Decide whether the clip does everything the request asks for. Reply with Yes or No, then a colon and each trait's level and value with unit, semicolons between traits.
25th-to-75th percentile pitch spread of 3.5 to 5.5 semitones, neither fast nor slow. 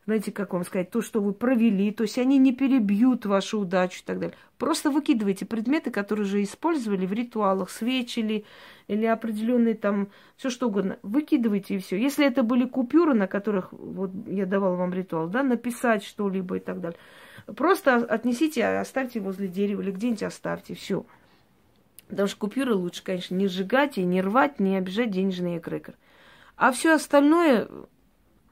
No: average, 4.6 semitones; fast, 165 wpm